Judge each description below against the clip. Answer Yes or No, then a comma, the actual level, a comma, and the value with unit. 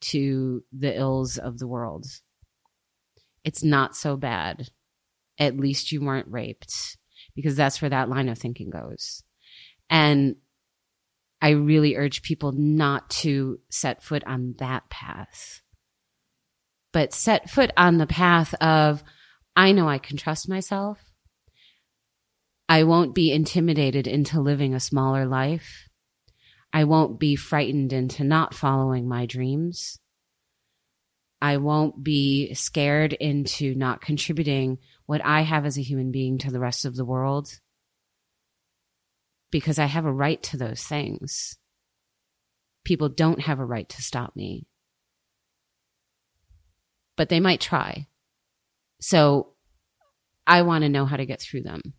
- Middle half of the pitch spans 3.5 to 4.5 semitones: No, average, 3.0 semitones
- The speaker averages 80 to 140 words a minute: Yes, slow, 135 wpm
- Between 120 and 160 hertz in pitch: Yes, medium, 140 Hz